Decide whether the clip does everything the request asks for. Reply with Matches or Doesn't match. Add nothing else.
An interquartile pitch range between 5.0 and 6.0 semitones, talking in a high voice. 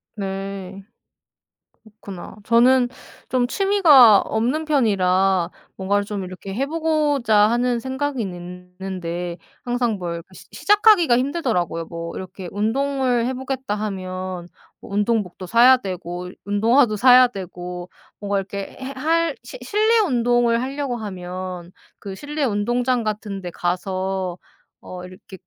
Matches